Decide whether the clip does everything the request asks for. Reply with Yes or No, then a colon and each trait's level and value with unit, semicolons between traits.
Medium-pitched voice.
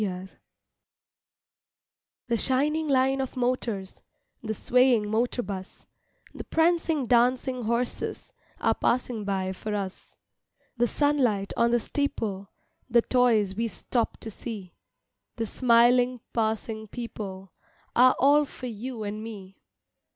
No: high, 235 Hz